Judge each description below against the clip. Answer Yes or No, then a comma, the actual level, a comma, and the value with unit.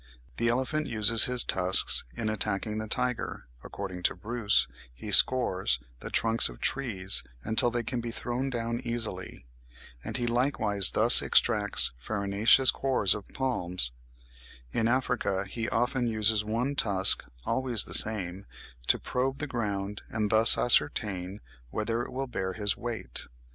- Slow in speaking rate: No, average, 150 wpm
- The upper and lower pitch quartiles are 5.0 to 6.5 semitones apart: No, average, 3.5 semitones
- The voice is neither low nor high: No, low, 110 Hz